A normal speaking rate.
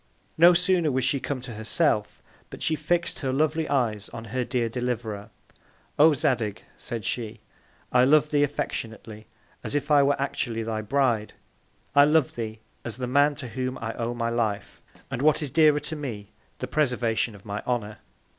Yes: average, 185 wpm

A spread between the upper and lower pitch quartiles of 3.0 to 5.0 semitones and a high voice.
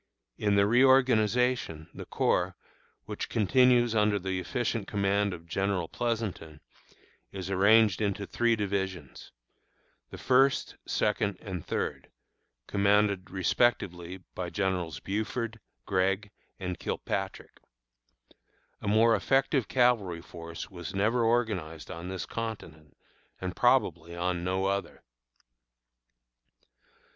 No: average, 3.8 semitones; low, 100 Hz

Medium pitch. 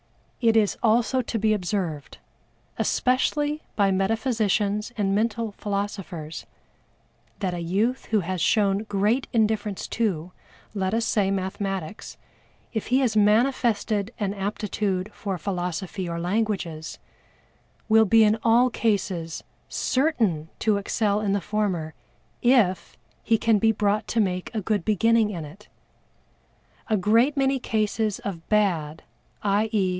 No: high, 210 Hz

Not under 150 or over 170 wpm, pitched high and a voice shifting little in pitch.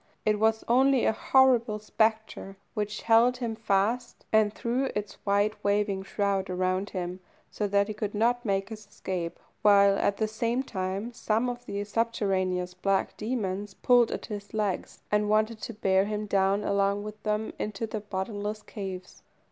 Yes: average, 165 wpm; high, 210 Hz; narrow, 2.1 semitones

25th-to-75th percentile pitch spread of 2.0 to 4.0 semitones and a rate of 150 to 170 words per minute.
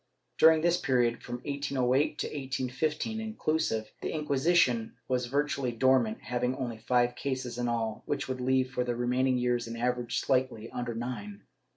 Yes: narrow, 2.4 semitones; average, 165 wpm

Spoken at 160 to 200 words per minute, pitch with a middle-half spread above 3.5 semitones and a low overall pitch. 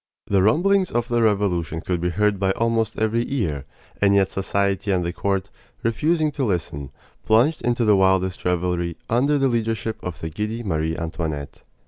Yes: average, 170 wpm; average, 4.6 semitones; low, 100 Hz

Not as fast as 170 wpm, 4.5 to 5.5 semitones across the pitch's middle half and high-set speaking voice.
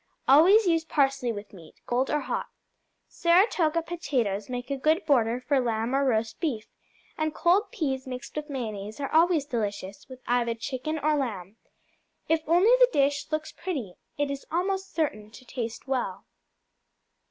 Yes: average, 160 wpm; average, 5.2 semitones; very high, 275 Hz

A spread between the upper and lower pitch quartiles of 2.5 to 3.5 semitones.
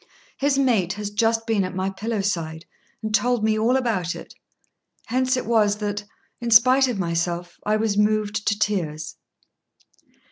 Yes: average, 3.2 semitones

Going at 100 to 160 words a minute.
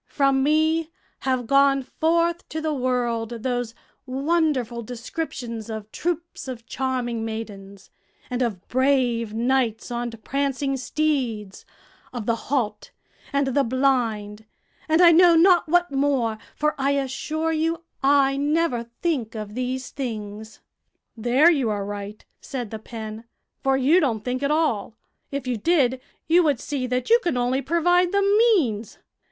Yes: average, 145 wpm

